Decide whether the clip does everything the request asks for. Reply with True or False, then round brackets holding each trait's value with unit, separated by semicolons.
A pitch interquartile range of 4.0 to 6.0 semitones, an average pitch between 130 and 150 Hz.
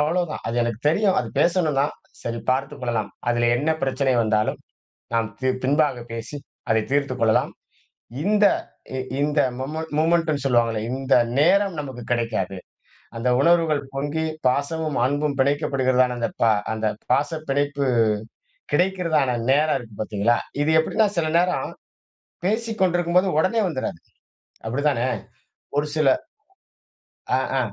True (4.7 semitones; 140 Hz)